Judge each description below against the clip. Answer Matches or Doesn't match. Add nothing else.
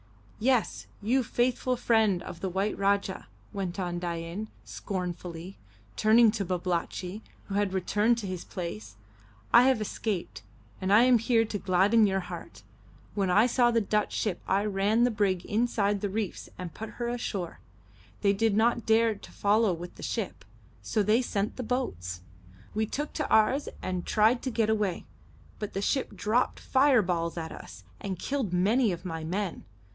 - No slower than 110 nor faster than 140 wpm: Doesn't match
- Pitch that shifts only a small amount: Doesn't match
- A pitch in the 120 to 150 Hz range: Doesn't match